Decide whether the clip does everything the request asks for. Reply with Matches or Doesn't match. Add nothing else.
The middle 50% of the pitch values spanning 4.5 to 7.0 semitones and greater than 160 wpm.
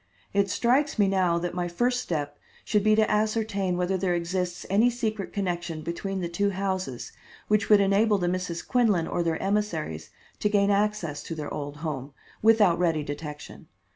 Doesn't match